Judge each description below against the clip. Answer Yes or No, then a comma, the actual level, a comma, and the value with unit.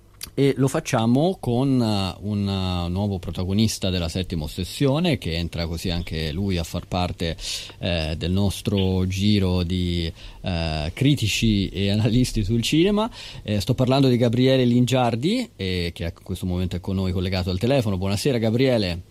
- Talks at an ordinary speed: Yes, average, 150 wpm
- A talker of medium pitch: No, low, 100 Hz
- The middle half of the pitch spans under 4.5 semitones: No, average, 5.3 semitones